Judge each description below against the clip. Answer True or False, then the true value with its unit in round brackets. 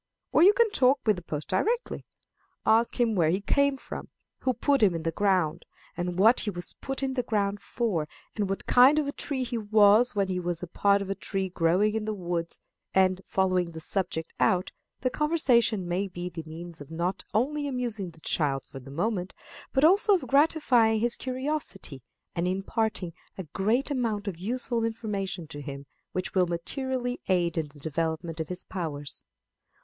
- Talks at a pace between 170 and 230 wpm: True (190 wpm)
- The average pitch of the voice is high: True (200 Hz)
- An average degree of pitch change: False (6.0 semitones)